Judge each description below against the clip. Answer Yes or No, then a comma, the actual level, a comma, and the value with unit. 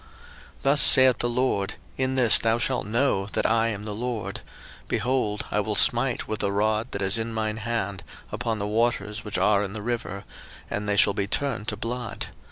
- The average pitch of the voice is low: Yes, low, 110 Hz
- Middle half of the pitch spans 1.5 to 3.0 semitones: Yes, narrow, 2.6 semitones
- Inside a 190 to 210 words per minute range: Yes, average, 200 wpm